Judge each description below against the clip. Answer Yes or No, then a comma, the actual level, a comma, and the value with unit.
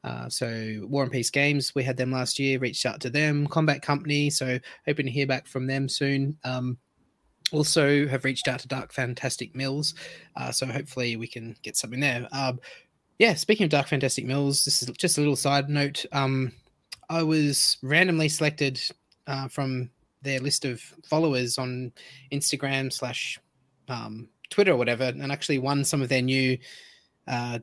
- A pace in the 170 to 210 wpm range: Yes, average, 180 wpm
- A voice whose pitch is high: No, low, 135 Hz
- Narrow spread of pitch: Yes, narrow, 2.2 semitones